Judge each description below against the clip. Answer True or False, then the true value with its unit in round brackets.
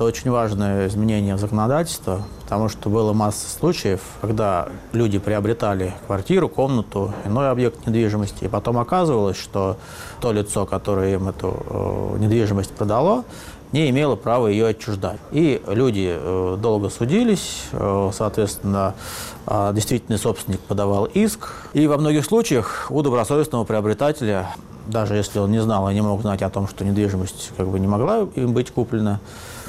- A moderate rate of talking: True (145 wpm)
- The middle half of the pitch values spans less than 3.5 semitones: True (3.0 semitones)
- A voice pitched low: True (105 Hz)